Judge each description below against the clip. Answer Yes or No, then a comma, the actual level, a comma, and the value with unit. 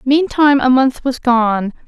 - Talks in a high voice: Yes, very high, 260 Hz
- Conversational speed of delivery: Yes, average, 160 wpm